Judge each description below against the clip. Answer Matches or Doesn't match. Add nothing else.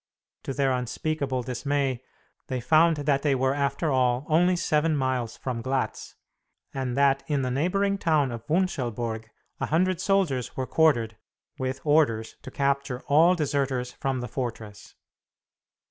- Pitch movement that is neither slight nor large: Matches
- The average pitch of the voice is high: Doesn't match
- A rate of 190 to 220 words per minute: Doesn't match